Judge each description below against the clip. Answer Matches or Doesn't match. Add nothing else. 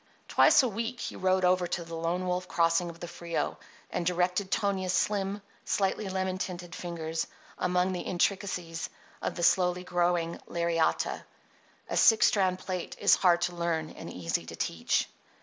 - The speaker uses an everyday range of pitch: Doesn't match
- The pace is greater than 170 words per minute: Doesn't match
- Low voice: Doesn't match